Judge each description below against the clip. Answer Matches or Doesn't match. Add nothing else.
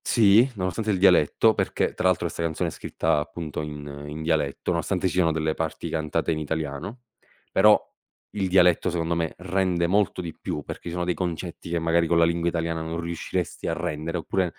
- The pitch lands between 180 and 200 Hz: Doesn't match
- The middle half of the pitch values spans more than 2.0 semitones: Matches